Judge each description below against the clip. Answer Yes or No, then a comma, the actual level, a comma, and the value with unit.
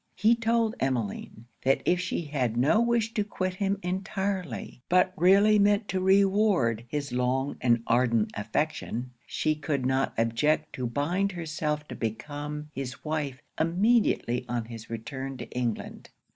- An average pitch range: No, wide, 7.5 semitones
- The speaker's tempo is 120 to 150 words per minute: Yes, average, 145 wpm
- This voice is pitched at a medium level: Yes, medium, 150 Hz